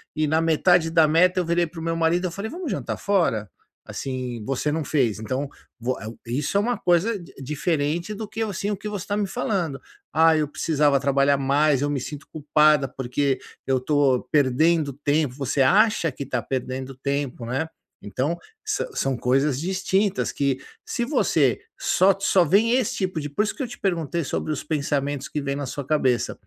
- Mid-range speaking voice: Yes, medium, 150 Hz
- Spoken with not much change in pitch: No, average, 4.8 semitones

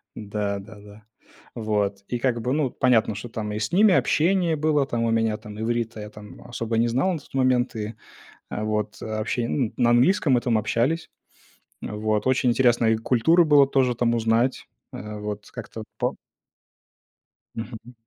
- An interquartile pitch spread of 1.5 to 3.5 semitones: Yes, average, 3.2 semitones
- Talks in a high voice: No, low, 115 Hz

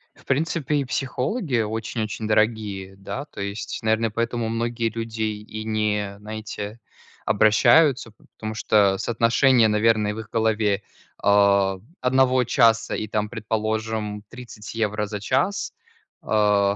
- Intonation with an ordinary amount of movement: No, narrow, 1.8 semitones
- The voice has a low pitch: Yes, low, 110 Hz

